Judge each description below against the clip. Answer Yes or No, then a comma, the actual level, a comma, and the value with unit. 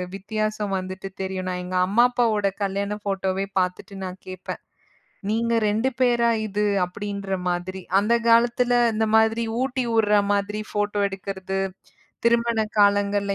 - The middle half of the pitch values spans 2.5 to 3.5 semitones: Yes, average, 2.9 semitones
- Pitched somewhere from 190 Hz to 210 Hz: Yes, high, 205 Hz